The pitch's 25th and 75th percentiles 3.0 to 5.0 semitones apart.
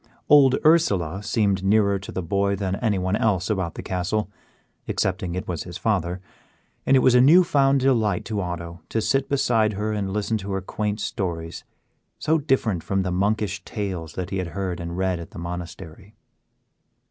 Yes: average, 3.3 semitones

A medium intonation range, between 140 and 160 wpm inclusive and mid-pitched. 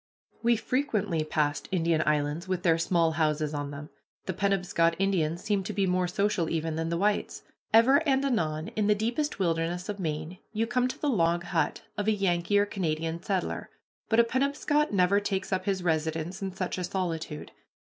No: average, 4.1 semitones; average, 185 wpm; medium, 180 Hz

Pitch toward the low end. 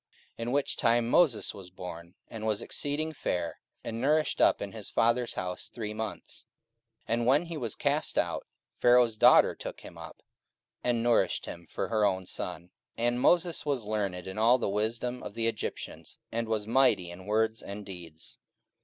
Yes: low, 110 Hz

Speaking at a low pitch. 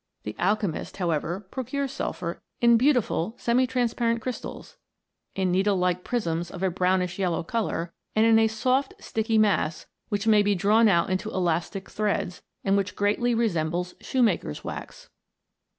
No: high, 205 Hz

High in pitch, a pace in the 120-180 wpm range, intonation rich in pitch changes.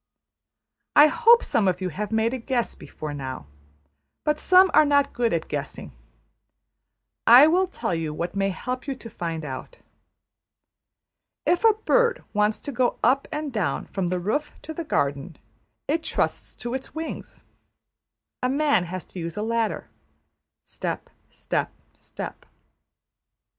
Yes: high, 230 Hz; average, 150 wpm; wide, 9.0 semitones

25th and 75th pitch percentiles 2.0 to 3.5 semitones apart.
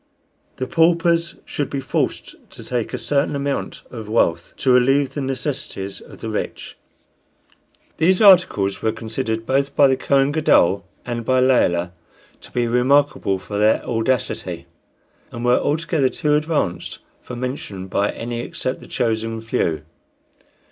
No: average, 4.2 semitones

